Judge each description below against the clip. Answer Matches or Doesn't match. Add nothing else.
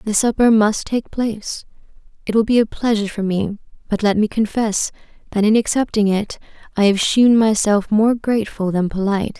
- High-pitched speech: Matches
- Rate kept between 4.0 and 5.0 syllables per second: Doesn't match